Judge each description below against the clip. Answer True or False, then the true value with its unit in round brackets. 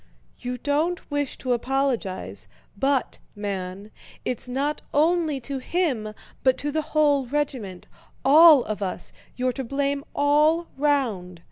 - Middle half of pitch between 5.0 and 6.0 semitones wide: False (3.8 semitones)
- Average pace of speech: False (120 wpm)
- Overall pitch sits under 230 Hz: False (275 Hz)